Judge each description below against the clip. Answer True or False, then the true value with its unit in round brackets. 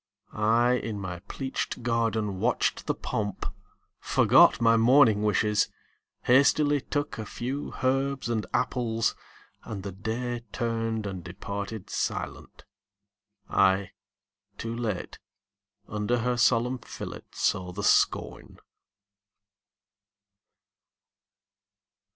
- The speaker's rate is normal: False (95 wpm)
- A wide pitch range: False (3.1 semitones)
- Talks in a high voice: False (115 Hz)